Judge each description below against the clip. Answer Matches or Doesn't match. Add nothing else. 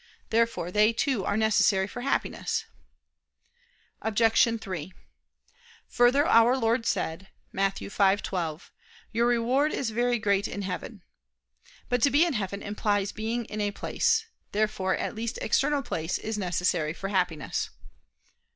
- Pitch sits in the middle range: Doesn't match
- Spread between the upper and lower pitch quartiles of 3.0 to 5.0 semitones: Matches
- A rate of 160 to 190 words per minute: Doesn't match